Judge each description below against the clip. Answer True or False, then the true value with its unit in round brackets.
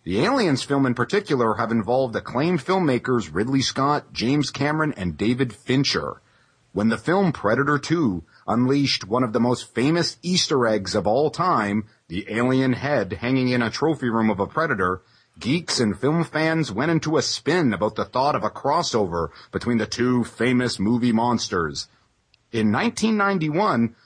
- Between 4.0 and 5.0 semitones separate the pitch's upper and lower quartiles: True (4.3 semitones)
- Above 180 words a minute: False (160 wpm)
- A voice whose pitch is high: False (125 Hz)